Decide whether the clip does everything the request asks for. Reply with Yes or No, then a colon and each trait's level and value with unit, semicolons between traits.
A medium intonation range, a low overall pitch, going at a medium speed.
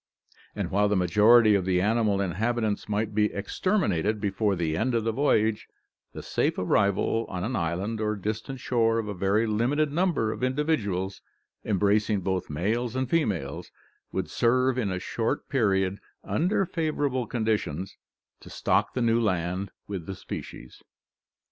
Yes: average, 3.6 semitones; low, 105 Hz; average, 155 wpm